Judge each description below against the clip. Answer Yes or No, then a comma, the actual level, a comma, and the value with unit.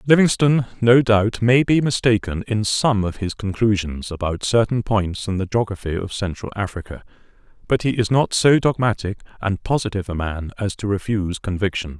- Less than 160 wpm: No, average, 170 wpm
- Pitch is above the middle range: No, low, 105 Hz